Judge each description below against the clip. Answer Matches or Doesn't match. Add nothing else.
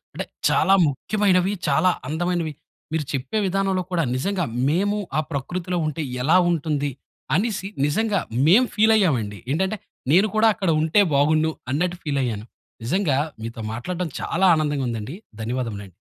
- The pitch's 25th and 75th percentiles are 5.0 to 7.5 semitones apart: Matches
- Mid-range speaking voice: Matches